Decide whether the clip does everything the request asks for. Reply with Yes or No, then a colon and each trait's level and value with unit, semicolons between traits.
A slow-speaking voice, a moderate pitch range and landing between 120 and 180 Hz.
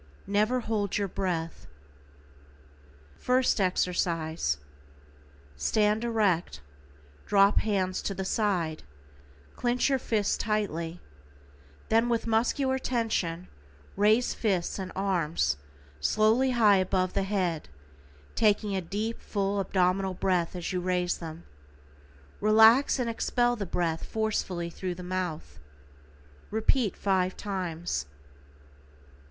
No: slow, 105 wpm; average, 3.7 semitones; high, 195 Hz